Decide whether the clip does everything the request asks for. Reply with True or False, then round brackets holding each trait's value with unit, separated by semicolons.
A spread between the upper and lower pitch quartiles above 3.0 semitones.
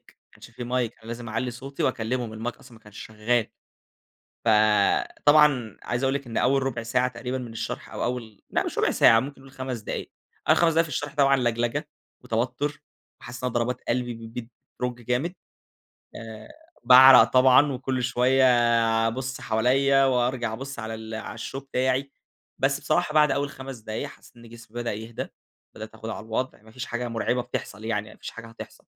False (2.7 semitones)